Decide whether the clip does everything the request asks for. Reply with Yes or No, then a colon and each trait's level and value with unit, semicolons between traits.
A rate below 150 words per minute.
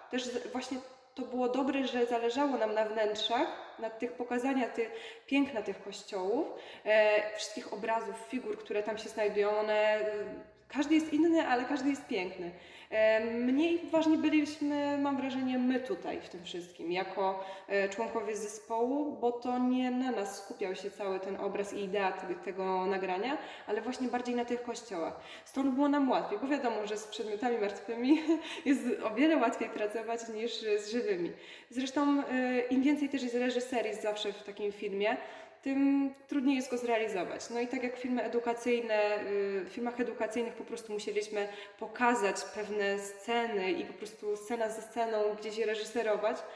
No: average, 155 wpm